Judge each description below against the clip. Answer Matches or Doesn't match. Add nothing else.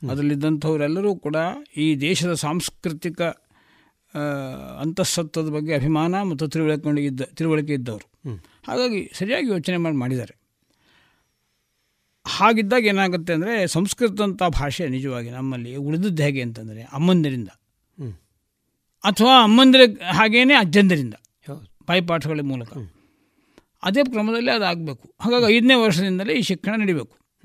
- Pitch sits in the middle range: Matches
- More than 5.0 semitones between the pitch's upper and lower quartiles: Matches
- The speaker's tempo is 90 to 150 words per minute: Matches